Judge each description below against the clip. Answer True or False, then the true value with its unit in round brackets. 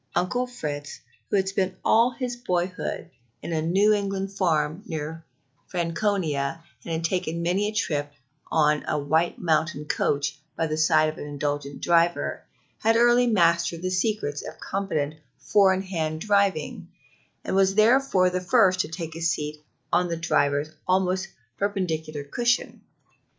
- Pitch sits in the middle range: True (175 Hz)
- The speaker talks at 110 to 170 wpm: True (145 wpm)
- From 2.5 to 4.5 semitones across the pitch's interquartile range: True (4.0 semitones)